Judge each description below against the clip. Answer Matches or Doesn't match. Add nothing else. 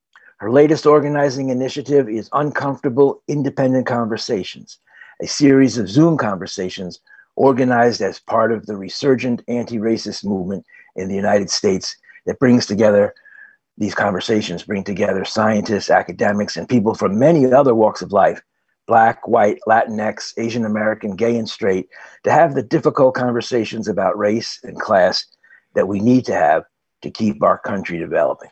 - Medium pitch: Doesn't match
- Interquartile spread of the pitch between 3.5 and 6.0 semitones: Matches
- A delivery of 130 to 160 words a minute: Matches